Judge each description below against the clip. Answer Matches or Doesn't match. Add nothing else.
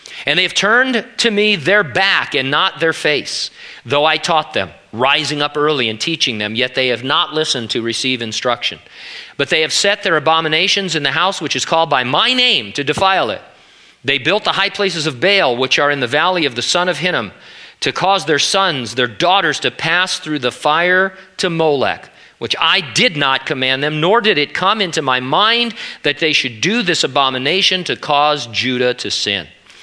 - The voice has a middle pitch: Matches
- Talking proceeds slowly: Doesn't match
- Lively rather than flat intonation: Matches